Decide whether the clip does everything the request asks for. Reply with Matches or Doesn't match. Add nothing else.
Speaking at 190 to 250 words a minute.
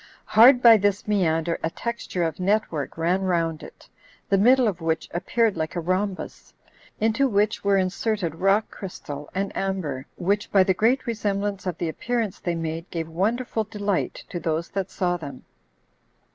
Doesn't match